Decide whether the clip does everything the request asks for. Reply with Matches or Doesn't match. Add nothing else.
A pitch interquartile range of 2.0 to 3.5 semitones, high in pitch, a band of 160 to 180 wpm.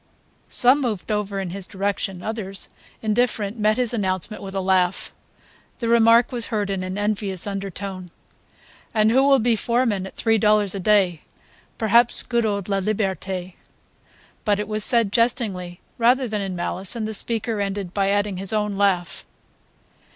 Matches